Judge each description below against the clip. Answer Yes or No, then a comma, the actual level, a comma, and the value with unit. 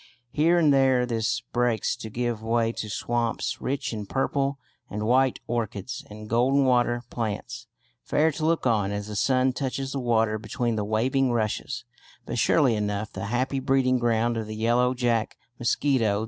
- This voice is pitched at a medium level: No, low, 120 Hz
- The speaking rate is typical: Yes, average, 170 wpm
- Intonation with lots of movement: No, average, 3.1 semitones